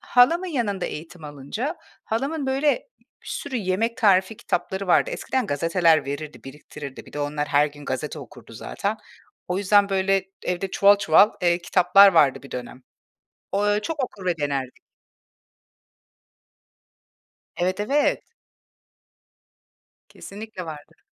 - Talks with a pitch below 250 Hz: Yes, medium, 185 Hz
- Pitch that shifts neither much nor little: No, wide, 6.5 semitones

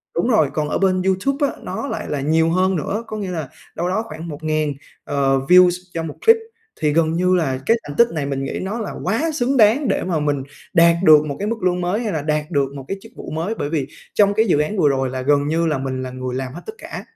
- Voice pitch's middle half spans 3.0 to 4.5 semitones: No, average, 5.3 semitones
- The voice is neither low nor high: Yes, medium, 165 Hz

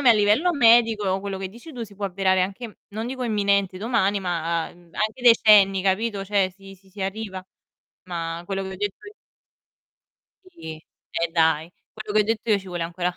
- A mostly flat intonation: No, average, 3.0 semitones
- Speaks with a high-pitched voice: Yes, high, 195 Hz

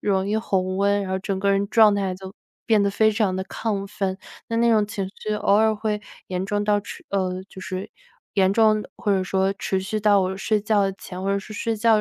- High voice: Yes, high, 200 Hz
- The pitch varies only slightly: Yes, narrow, 1.9 semitones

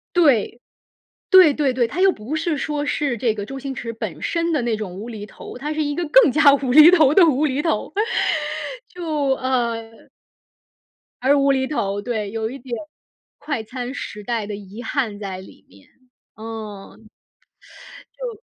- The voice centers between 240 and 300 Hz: Yes, very high, 260 Hz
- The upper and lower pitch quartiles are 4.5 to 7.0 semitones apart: Yes, average, 5.2 semitones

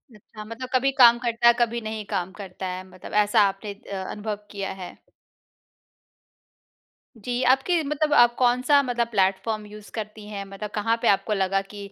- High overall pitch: Yes, high, 215 Hz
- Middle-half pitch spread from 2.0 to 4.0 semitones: Yes, average, 3.3 semitones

